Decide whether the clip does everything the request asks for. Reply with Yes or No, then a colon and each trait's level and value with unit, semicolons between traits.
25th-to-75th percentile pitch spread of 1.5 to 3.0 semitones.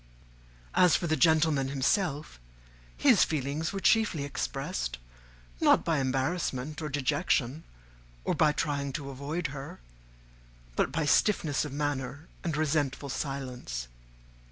Yes: average, 2.7 semitones